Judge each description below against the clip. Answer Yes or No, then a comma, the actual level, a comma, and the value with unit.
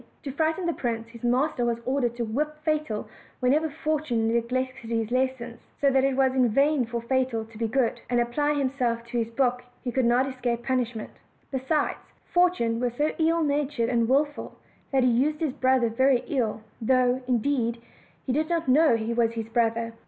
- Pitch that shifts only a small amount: No, average, 3.3 semitones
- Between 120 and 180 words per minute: No, average, 190 wpm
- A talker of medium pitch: No, very high, 255 Hz